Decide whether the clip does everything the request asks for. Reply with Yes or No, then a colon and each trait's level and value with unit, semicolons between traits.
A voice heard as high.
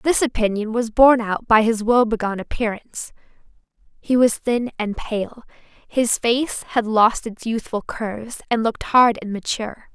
Yes: high, 225 Hz